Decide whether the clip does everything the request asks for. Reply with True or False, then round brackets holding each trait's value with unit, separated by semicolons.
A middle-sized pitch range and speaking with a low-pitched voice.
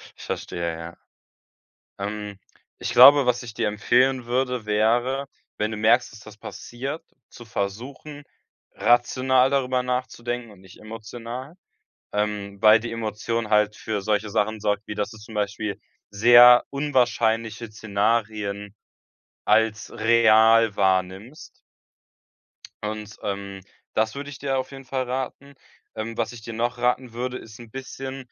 True (3.0 semitones; 115 Hz)